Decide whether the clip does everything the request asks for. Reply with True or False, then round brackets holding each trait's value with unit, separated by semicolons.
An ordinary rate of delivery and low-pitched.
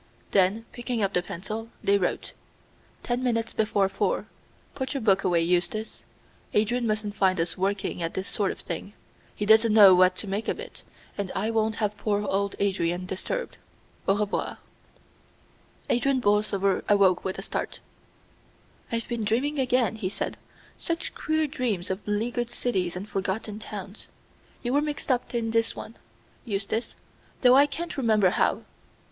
False (160 wpm; 210 Hz)